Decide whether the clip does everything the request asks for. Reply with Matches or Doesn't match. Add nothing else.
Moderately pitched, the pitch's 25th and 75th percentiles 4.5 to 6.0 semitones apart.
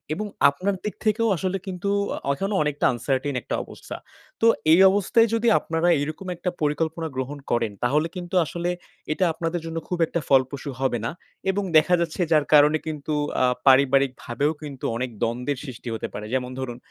Matches